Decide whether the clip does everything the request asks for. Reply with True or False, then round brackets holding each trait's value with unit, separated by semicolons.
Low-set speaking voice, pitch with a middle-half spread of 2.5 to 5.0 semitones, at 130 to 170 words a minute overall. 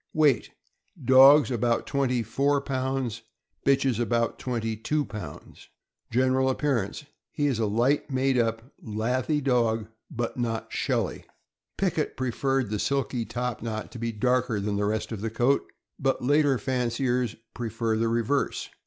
True (125 Hz; 3.0 semitones; 150 wpm)